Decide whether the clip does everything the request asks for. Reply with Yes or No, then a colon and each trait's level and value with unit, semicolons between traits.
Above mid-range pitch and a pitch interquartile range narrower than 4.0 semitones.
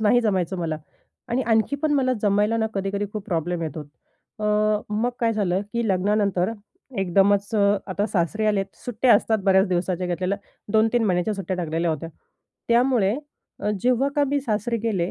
Yes: high, 205 Hz; average, 3.6 semitones